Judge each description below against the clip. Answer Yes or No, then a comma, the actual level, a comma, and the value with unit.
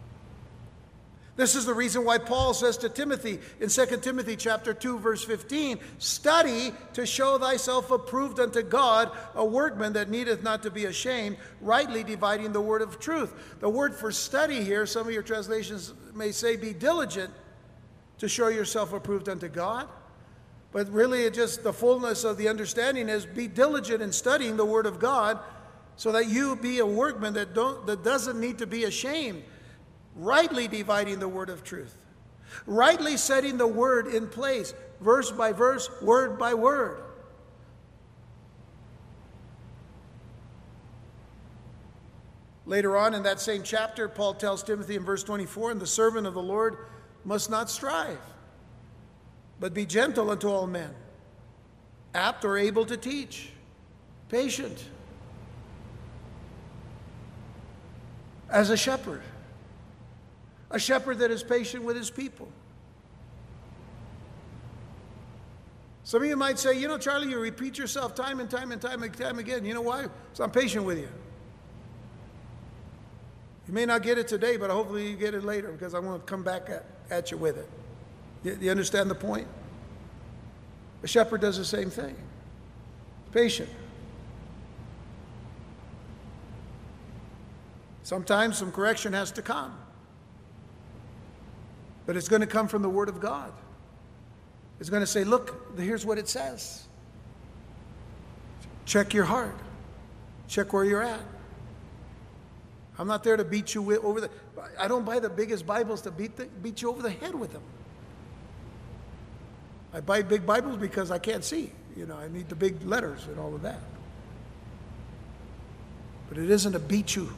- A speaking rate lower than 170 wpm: Yes, average, 150 wpm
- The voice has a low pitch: No, high, 210 Hz